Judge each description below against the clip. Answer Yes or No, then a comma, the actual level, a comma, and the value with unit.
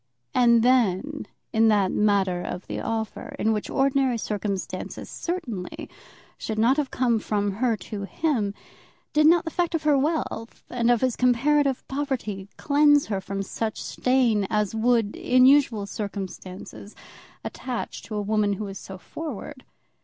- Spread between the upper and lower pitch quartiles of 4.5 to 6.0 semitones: Yes, average, 4.8 semitones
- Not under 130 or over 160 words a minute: Yes, average, 155 wpm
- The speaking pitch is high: Yes, high, 230 Hz